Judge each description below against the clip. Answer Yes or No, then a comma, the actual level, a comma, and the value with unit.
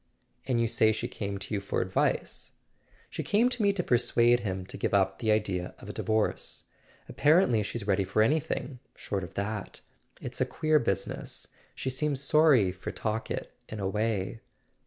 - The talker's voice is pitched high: No, low, 110 Hz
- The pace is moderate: Yes, average, 180 wpm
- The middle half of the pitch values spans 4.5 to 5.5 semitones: Yes, average, 5.0 semitones